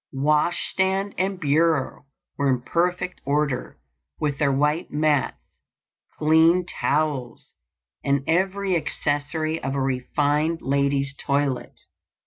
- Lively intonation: No, average, 3.2 semitones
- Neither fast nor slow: No, slow, 110 wpm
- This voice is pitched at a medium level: Yes, medium, 150 Hz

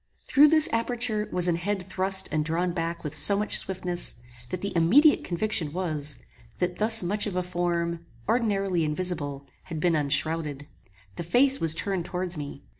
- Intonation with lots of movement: No, average, 3.7 semitones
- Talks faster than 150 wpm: Yes, average, 170 wpm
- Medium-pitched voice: Yes, medium, 180 Hz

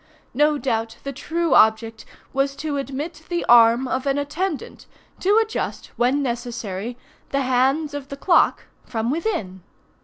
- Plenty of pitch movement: No, average, 4.1 semitones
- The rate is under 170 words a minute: Yes, average, 145 wpm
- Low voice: No, very high, 275 Hz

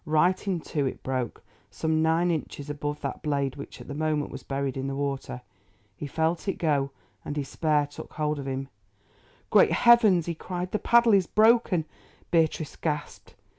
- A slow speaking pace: No, average, 175 wpm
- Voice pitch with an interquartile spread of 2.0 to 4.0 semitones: Yes, average, 3.7 semitones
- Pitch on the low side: No, medium, 155 Hz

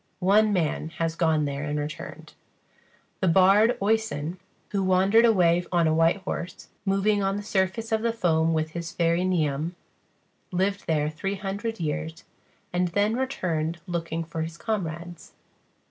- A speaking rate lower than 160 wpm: Yes, average, 150 wpm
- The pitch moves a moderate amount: Yes, average, 3.7 semitones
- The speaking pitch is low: No, medium, 175 Hz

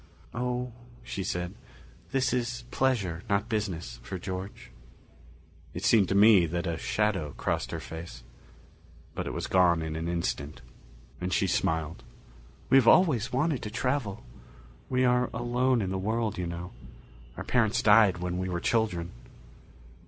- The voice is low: Yes, low, 100 Hz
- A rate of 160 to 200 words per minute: No, average, 150 wpm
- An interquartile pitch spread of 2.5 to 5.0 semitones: No, wide, 5.6 semitones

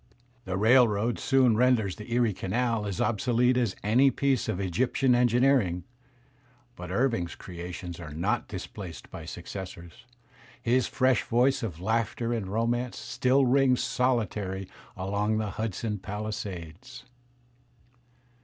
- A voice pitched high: No, low, 110 Hz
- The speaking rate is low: Yes, slow, 120 wpm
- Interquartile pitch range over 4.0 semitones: Yes, average, 4.6 semitones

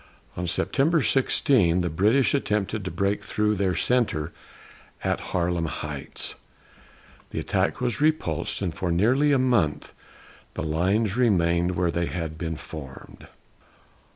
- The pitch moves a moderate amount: No, wide, 5.8 semitones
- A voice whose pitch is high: No, very low, 95 Hz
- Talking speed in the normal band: No, slow, 130 wpm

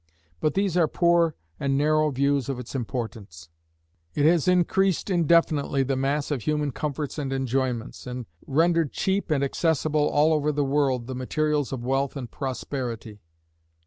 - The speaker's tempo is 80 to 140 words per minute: No, average, 155 wpm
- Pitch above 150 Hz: No, medium, 140 Hz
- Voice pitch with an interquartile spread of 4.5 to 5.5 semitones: No, average, 2.9 semitones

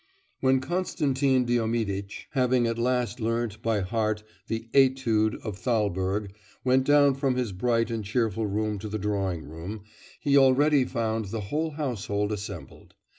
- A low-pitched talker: Yes, low, 115 Hz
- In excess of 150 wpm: No, average, 145 wpm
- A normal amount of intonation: Yes, average, 3.9 semitones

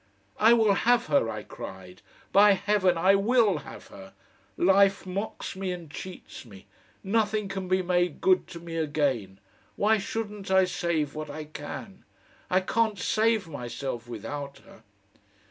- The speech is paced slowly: No, average, 150 wpm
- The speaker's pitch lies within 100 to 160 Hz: No, medium, 185 Hz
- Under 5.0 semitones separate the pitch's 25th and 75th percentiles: No, wide, 5.5 semitones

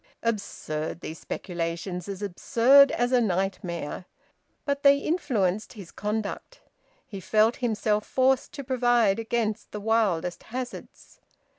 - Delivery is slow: Yes, slow, 120 wpm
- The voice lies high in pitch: Yes, high, 215 Hz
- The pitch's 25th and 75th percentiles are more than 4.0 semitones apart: Yes, average, 4.5 semitones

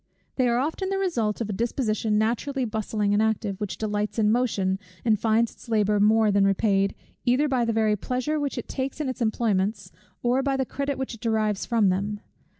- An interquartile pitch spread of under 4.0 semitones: Yes, average, 3.3 semitones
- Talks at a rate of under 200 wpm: No, fast, 205 wpm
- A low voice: No, high, 220 Hz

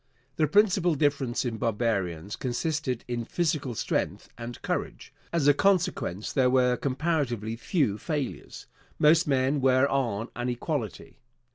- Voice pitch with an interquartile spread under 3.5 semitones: No, average, 4.3 semitones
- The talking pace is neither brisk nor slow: No, slow, 130 wpm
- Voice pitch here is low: Yes, low, 130 Hz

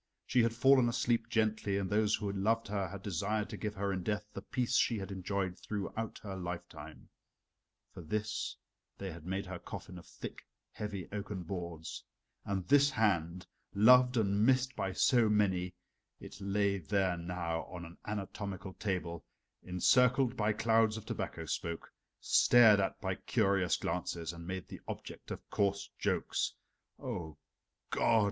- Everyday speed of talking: Yes, average, 155 wpm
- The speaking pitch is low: Yes, low, 100 Hz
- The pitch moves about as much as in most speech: Yes, average, 3.3 semitones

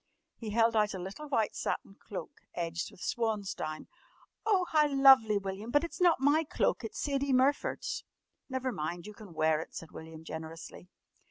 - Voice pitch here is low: No, high, 220 Hz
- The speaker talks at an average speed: Yes, average, 170 wpm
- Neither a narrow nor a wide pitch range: No, wide, 8.0 semitones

